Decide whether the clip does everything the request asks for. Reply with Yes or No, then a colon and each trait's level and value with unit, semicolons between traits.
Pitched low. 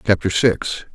Yes: very low, 95 Hz